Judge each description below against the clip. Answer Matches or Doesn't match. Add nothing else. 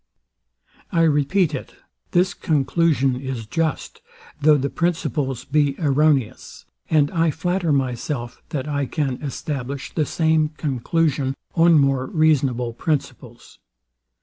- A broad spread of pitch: Doesn't match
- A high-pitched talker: Doesn't match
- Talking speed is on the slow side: Matches